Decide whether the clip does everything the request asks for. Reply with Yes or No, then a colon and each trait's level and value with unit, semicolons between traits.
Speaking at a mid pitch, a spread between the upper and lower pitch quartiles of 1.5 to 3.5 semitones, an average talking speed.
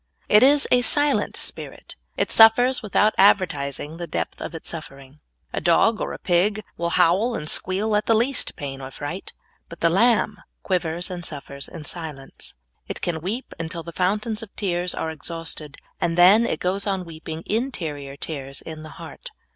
No: medium, 175 Hz; average, 5.1 semitones; average, 180 wpm